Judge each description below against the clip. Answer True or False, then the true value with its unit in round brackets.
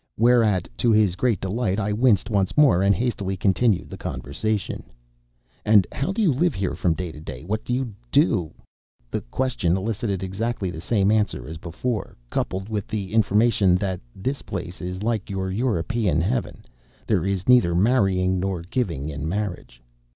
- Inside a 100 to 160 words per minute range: False (170 wpm)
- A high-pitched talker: False (100 Hz)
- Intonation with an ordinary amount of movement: True (3.8 semitones)